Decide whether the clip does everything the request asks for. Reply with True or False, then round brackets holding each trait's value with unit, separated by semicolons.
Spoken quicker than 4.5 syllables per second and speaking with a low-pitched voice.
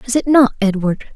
False (6.0 syllables/s; 235 Hz)